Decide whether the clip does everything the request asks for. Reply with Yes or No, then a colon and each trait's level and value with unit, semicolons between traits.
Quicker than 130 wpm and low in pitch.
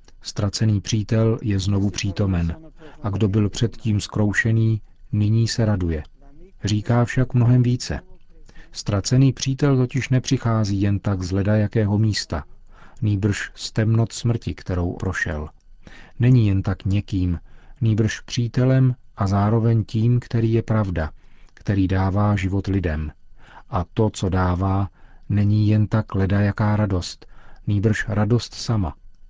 No: average, 125 wpm; low, 105 Hz